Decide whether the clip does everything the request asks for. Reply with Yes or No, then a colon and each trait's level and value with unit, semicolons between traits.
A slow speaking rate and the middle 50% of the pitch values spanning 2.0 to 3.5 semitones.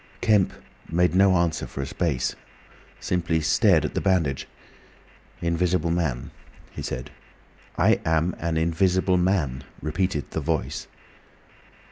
Yes: slow, 120 wpm; average, 2.7 semitones